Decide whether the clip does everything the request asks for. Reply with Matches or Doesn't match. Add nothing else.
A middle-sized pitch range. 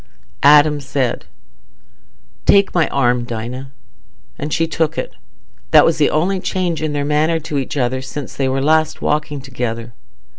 Matches